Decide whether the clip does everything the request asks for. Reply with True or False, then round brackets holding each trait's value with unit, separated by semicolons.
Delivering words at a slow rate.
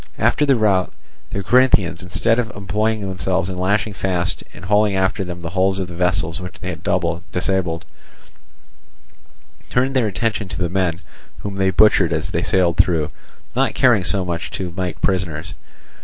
False (170 wpm)